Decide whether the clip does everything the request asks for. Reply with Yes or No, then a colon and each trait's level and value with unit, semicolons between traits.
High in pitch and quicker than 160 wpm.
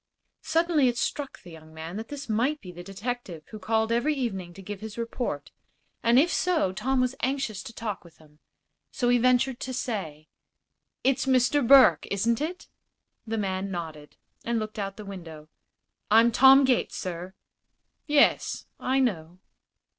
Yes: high, 225 Hz; average, 170 wpm